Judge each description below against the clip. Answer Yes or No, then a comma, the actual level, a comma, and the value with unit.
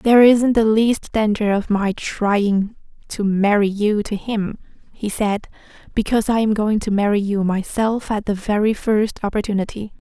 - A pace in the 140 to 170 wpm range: Yes, average, 165 wpm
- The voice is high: Yes, high, 210 Hz